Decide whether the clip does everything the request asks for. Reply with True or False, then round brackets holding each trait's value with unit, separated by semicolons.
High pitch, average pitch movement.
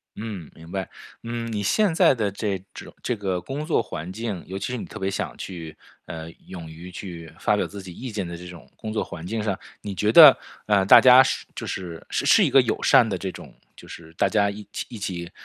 False (100 Hz; 4.1 semitones)